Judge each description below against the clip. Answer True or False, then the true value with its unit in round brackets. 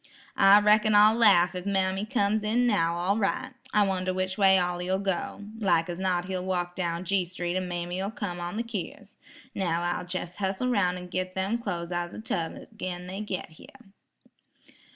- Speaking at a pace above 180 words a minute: True (195 wpm)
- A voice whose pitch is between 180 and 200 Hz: True (190 Hz)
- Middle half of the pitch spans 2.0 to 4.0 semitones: True (2.7 semitones)